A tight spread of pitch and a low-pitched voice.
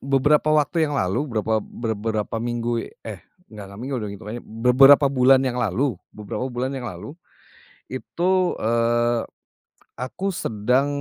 No: average, 3.7 semitones; low, 120 Hz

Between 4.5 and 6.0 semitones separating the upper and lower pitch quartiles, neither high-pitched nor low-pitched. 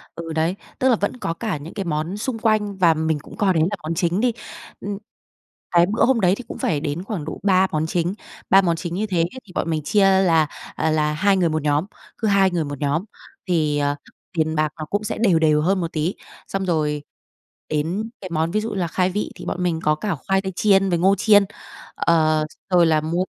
No: average, 3.9 semitones; medium, 175 Hz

